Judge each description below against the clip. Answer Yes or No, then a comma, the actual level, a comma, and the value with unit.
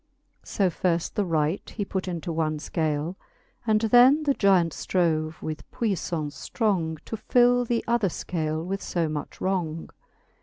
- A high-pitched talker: No, medium, 180 Hz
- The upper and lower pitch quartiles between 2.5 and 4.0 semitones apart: No, average, 5.1 semitones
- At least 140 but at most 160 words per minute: Yes, average, 150 wpm